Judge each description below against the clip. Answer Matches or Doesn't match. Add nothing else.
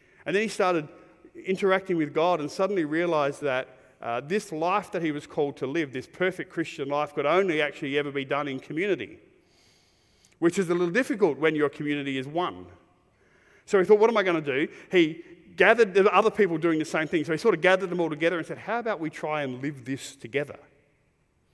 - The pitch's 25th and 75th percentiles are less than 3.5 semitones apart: Doesn't match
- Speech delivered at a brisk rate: Matches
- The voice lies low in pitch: Doesn't match